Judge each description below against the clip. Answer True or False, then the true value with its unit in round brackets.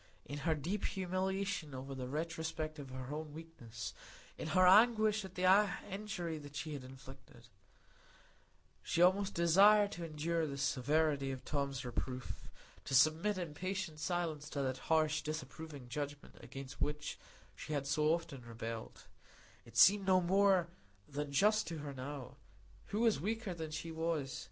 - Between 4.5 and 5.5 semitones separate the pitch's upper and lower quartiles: True (5.0 semitones)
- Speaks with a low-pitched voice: False (155 Hz)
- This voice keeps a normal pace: True (145 wpm)